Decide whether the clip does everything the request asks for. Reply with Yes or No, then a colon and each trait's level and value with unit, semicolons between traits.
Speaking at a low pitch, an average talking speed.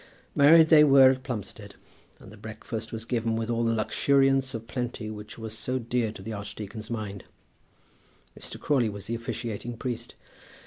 Yes: low, 115 Hz; average, 170 wpm